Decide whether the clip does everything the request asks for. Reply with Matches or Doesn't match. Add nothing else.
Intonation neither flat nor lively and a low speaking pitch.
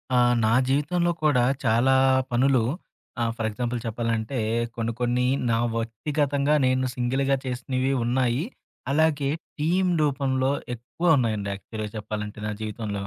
Matches